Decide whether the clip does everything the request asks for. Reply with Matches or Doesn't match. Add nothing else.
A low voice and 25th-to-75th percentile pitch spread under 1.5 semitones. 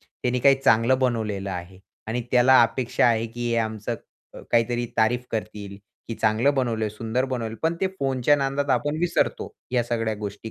Doesn't match